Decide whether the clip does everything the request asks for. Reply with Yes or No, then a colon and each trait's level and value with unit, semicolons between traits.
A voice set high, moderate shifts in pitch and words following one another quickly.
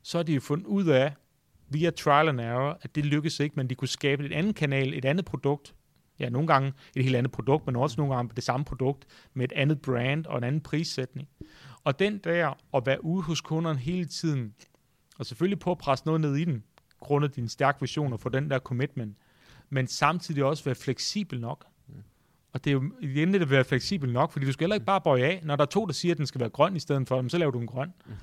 No: medium, 140 Hz; average, 3.3 semitones; fast, 250 wpm